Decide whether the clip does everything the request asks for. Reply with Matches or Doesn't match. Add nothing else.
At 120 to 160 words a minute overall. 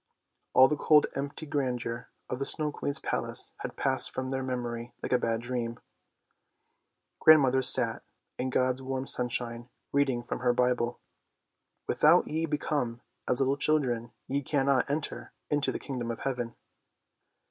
Matches